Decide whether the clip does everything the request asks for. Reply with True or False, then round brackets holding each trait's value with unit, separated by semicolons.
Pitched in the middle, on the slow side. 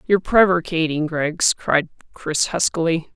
True (165 Hz; 115 wpm)